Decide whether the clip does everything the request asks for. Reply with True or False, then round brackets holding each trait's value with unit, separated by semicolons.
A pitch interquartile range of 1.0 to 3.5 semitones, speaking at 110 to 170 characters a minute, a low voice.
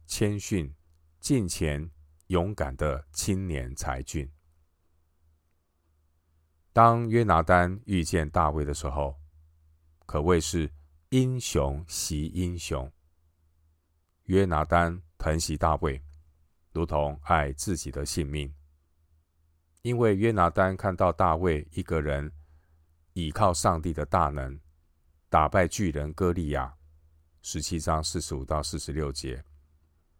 True (2.6 semitones; 165 characters per minute; 80 Hz)